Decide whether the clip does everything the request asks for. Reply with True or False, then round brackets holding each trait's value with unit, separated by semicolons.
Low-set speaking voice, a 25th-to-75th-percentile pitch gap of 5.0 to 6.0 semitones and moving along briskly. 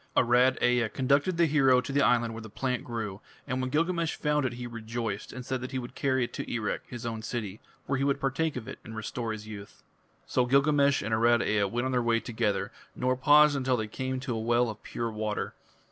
False (125 Hz; 3.0 semitones; 235 wpm)